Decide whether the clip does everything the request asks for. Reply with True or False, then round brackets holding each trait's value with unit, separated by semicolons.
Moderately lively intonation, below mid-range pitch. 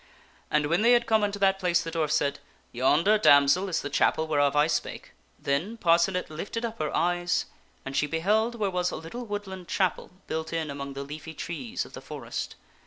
False (4.9 semitones; 170 Hz)